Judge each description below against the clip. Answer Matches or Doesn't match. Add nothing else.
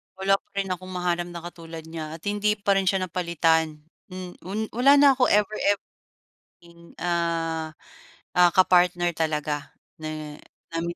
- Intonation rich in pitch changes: Doesn't match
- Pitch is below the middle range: Doesn't match